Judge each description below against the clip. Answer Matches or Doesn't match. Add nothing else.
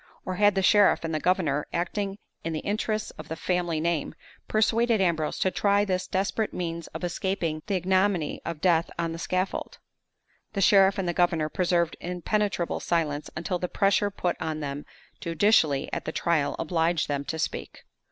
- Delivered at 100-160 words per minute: Doesn't match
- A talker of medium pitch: Matches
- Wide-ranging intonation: Doesn't match